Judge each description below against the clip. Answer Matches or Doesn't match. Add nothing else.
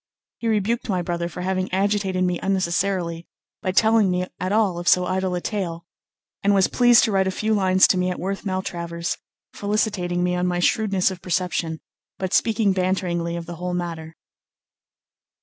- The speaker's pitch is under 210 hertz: Matches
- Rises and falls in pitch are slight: Matches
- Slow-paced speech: Doesn't match